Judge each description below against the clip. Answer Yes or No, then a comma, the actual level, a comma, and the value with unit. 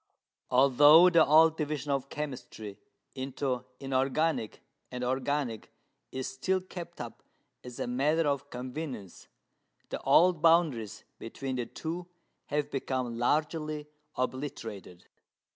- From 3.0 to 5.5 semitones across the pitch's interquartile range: Yes, average, 3.6 semitones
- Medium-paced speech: No, slow, 110 wpm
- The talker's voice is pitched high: No, medium, 140 Hz